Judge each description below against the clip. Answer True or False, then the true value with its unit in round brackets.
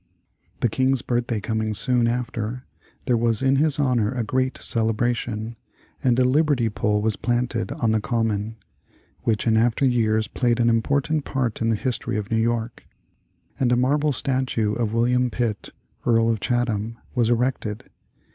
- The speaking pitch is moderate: False (120 Hz)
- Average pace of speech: True (160 wpm)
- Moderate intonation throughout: False (2.2 semitones)